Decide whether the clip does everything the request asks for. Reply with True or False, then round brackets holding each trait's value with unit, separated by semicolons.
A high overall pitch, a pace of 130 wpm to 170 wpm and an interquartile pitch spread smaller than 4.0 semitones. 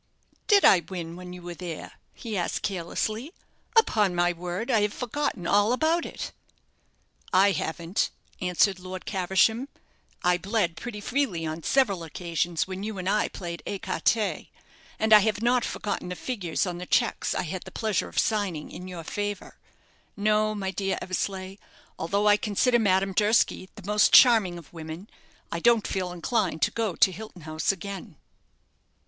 True (195 Hz; 165 wpm; 3.4 semitones)